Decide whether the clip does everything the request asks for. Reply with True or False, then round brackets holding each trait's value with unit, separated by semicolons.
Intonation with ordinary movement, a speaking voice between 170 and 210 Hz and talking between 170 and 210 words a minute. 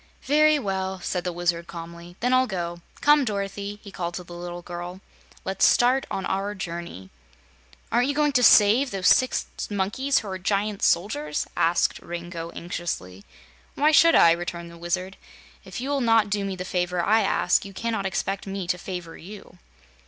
True (3.8 semitones; 190 Hz; 180 wpm)